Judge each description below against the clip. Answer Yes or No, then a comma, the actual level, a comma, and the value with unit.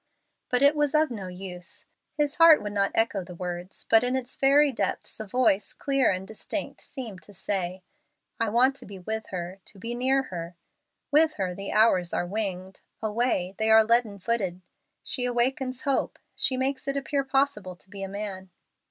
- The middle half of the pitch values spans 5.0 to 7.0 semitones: Yes, wide, 5.6 semitones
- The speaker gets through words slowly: No, average, 185 wpm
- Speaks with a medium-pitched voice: No, high, 220 Hz